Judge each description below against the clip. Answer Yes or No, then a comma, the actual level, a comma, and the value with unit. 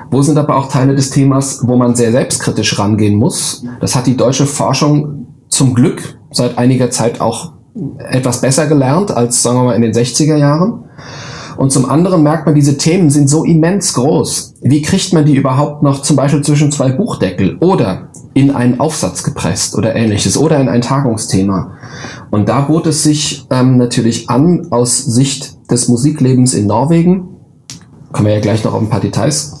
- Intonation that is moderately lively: Yes, average, 3.5 semitones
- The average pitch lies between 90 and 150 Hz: Yes, low, 135 Hz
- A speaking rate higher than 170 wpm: Yes, average, 185 wpm